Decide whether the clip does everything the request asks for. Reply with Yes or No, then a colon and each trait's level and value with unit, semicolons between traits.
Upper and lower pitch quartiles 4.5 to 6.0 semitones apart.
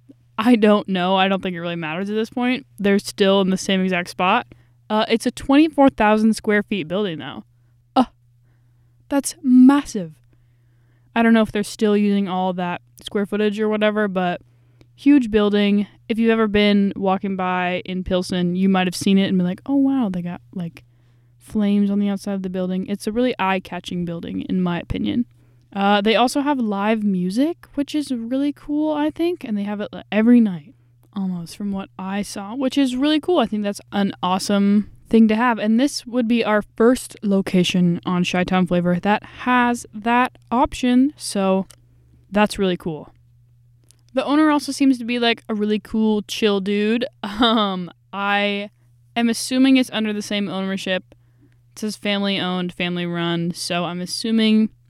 No: average, 4.1 semitones